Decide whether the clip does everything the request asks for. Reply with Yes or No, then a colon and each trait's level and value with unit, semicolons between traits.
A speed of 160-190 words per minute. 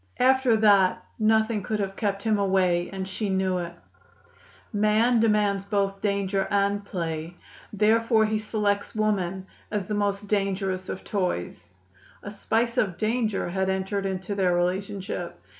No: average, 140 wpm